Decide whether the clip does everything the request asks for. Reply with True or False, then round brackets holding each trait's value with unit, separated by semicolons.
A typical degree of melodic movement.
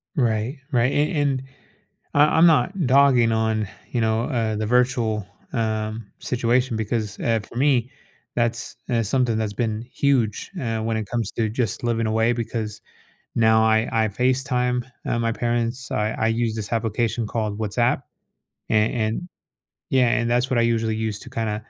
False (2.1 semitones)